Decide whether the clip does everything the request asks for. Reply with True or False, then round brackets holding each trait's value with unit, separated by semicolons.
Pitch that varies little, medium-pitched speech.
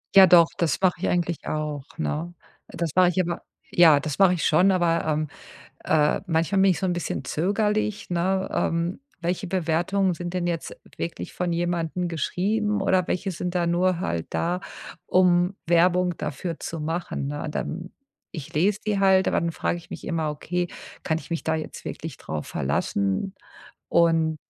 True (2.3 semitones; 175 Hz)